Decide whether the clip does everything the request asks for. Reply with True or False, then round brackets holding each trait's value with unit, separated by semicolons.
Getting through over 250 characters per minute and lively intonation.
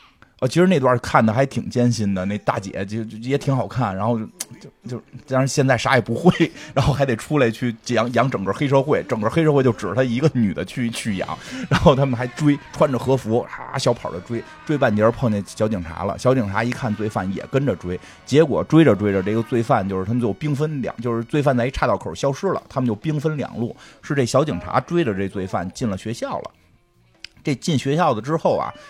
False (325 characters per minute; 4.0 semitones)